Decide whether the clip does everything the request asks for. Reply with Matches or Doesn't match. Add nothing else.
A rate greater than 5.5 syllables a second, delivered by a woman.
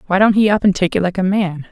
Matches